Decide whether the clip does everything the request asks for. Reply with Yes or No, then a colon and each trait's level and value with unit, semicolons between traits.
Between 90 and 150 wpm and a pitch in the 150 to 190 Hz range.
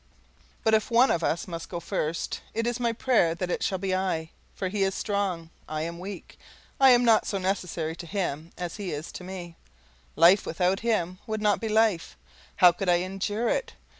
No: fast, 205 wpm; medium, 185 Hz